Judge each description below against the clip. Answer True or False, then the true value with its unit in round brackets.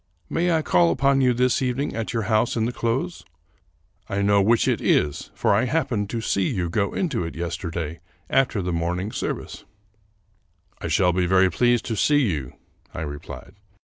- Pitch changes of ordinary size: False (5.8 semitones)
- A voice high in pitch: False (105 Hz)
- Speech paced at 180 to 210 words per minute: True (185 wpm)